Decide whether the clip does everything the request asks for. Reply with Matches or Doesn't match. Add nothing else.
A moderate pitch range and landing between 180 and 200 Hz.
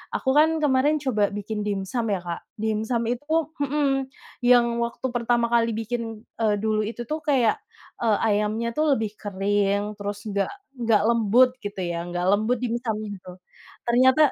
Doesn't match